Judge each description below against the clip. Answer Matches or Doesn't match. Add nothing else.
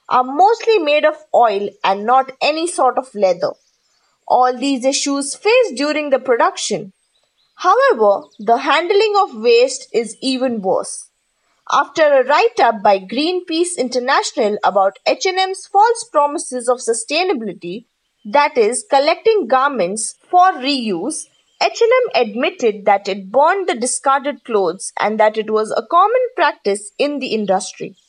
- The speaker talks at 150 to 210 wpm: Doesn't match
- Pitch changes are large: Matches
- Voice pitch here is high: Matches